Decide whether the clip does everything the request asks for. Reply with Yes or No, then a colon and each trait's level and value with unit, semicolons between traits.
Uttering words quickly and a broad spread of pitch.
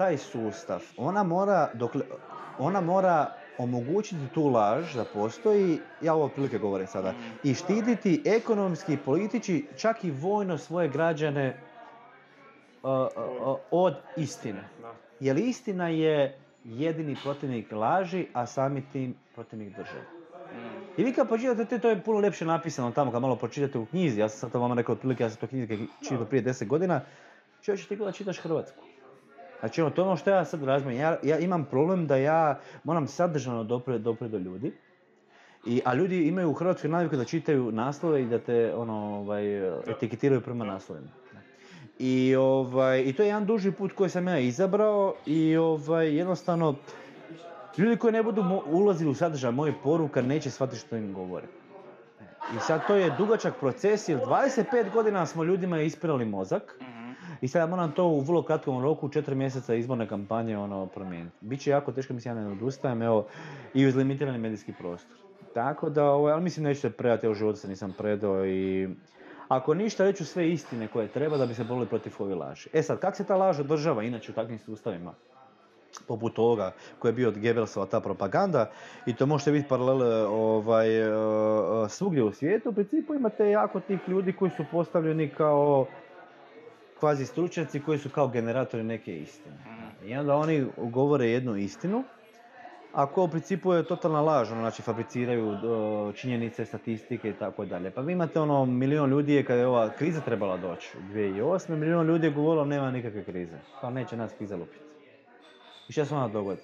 Yes: fast, 175 wpm; wide, 6.4 semitones